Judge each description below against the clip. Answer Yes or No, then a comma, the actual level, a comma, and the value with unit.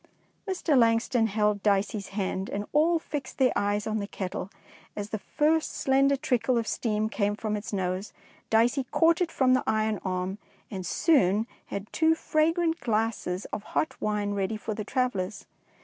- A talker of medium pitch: No, high, 220 Hz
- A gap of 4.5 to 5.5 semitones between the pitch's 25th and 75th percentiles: Yes, average, 4.8 semitones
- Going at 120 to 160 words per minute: No, average, 170 wpm